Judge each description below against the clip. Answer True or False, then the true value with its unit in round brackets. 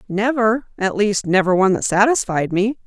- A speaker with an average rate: True (165 wpm)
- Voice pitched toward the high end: True (210 Hz)